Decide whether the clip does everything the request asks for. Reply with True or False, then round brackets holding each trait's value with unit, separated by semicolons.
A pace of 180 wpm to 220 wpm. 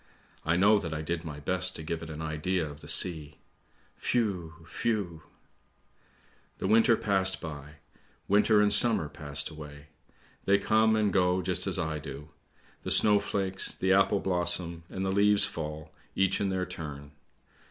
False (165 wpm)